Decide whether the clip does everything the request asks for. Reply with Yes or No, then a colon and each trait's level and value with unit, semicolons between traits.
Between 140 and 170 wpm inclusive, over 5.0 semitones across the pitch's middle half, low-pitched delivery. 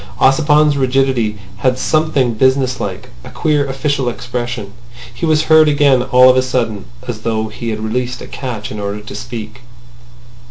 No: average, 165 wpm; average, 3.3 semitones; low, 125 Hz